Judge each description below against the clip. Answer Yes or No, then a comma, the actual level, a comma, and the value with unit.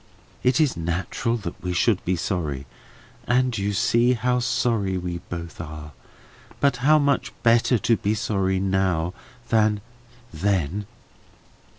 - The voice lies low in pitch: Yes, low, 100 Hz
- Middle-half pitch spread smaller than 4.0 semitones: No, average, 5.1 semitones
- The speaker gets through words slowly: Yes, slow, 130 wpm